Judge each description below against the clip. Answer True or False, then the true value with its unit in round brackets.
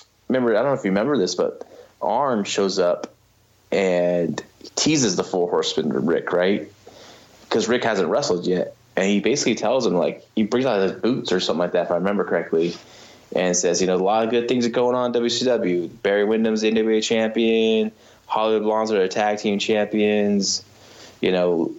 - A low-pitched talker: True (110 Hz)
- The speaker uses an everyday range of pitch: True (3.0 semitones)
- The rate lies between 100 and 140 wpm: False (195 wpm)